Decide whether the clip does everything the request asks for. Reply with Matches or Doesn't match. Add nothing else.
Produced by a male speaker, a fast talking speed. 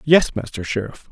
Doesn't match